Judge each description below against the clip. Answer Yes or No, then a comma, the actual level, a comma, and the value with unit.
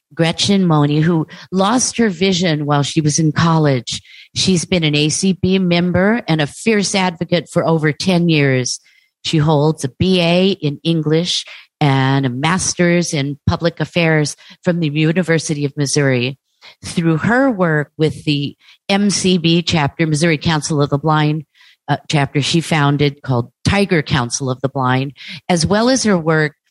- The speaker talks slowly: No, average, 155 wpm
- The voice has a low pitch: No, medium, 160 Hz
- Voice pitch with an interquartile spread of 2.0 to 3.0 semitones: No, average, 3.6 semitones